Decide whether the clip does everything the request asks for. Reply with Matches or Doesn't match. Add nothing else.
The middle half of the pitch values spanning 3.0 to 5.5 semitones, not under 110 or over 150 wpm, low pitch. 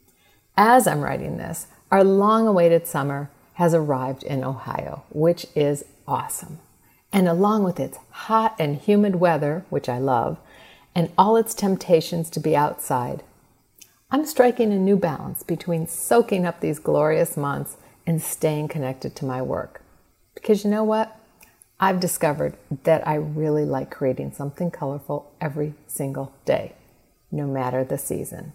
Doesn't match